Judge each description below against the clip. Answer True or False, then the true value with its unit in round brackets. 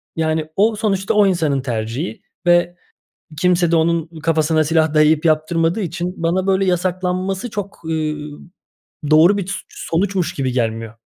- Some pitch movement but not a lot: True (3.1 semitones)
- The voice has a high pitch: False (170 Hz)